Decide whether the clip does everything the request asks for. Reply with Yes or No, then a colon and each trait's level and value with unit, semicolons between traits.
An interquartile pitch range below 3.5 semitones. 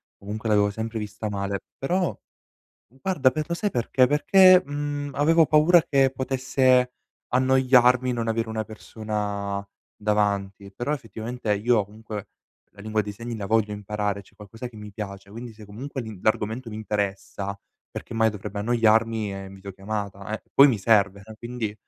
No: average, 3.8 semitones